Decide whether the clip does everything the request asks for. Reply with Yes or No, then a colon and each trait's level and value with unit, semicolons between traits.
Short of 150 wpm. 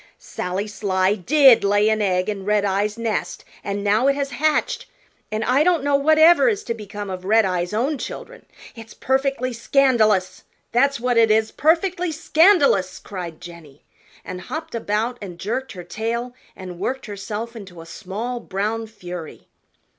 No: average, 155 wpm